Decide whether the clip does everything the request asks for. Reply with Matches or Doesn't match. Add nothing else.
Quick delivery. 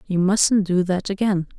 Doesn't match